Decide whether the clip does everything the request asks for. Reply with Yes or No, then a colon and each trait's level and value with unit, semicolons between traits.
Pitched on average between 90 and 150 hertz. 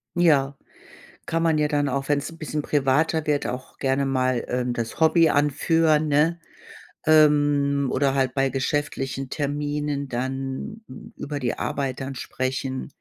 Yes: medium, 140 Hz